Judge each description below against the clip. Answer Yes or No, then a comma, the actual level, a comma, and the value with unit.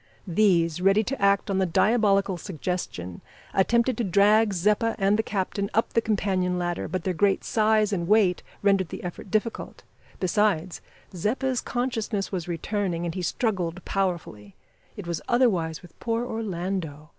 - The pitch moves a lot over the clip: No, average, 3.5 semitones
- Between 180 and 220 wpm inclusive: No, average, 155 wpm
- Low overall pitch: No, high, 195 Hz